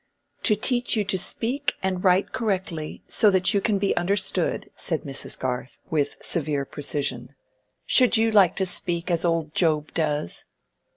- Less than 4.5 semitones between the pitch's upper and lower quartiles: No, average, 4.8 semitones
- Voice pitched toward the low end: No, medium, 180 Hz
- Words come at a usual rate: Yes, average, 160 wpm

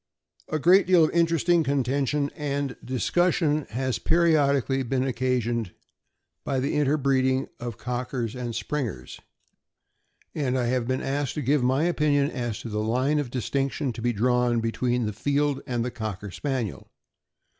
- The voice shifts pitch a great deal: No, average, 3.2 semitones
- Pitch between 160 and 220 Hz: No, low, 130 Hz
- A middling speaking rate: Yes, average, 150 wpm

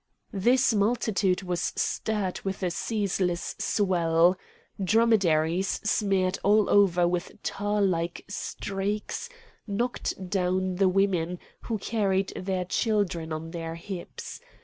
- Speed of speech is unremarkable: No, slow, 110 wpm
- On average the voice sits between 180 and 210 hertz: Yes, high, 190 Hz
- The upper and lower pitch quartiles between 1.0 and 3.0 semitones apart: Yes, narrow, 2.5 semitones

